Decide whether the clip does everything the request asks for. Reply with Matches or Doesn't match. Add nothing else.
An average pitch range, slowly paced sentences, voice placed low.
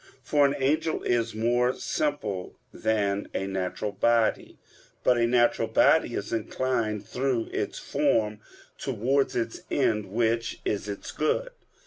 Matches